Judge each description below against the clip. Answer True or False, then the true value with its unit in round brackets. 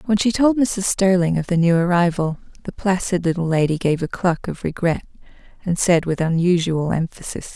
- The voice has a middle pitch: True (175 Hz)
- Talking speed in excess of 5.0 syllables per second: True (5.2 syllables/s)